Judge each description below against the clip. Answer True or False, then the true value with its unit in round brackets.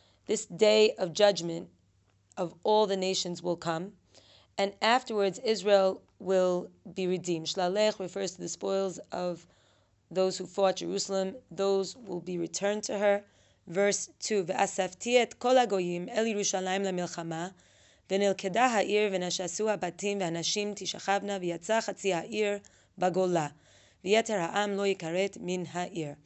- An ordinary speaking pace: False (125 wpm)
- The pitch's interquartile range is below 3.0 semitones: True (2.6 semitones)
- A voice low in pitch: False (190 Hz)